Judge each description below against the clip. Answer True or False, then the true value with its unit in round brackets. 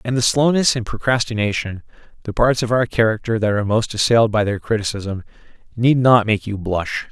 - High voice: False (110 Hz)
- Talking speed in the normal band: True (185 wpm)